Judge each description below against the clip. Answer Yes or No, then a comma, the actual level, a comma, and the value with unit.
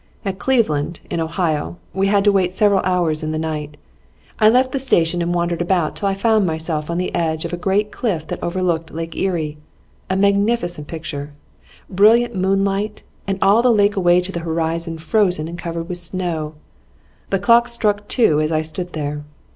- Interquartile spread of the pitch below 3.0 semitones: No, average, 3.8 semitones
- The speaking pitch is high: No, medium, 175 Hz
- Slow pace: No, average, 190 wpm